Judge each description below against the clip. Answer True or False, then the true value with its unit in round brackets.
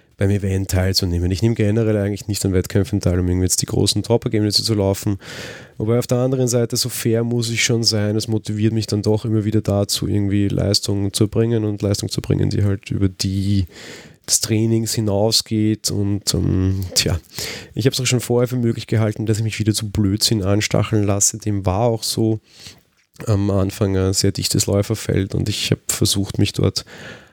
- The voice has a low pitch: True (105 Hz)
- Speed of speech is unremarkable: False (195 wpm)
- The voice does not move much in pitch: True (2.3 semitones)